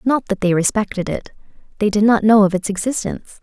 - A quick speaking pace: Yes, fast, 210 wpm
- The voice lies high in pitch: Yes, high, 210 Hz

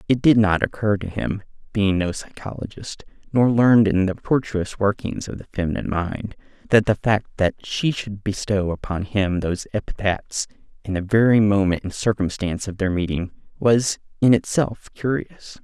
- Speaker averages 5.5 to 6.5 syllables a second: No, 5.0 syllables/s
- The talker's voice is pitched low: Yes, low, 100 Hz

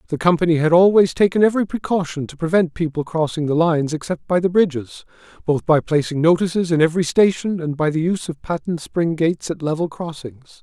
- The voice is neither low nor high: Yes, medium, 165 Hz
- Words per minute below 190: No, average, 200 wpm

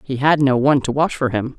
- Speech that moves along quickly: Yes, fast, 305 wpm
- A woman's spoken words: Yes, female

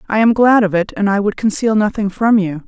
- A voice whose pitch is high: Yes, high, 210 Hz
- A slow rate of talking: No, fast, 270 wpm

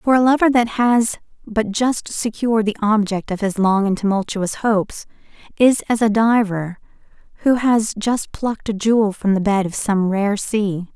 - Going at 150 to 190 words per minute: Yes, average, 180 wpm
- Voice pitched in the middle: No, high, 215 Hz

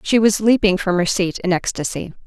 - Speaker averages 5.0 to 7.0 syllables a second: Yes, 5.3 syllables/s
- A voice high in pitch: Yes, high, 195 Hz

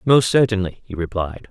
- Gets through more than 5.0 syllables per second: Yes, 5.2 syllables/s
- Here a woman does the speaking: No, male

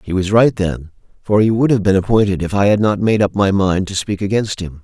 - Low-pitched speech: Yes, low, 100 Hz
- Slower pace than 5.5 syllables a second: No, 5.7 syllables/s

